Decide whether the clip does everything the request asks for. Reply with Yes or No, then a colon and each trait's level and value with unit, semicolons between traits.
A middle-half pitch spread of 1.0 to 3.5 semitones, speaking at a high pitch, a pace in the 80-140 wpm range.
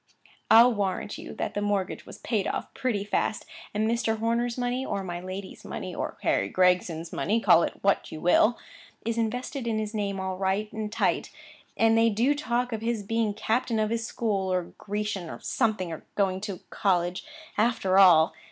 No: average, 3.2 semitones; high, 210 Hz; average, 180 wpm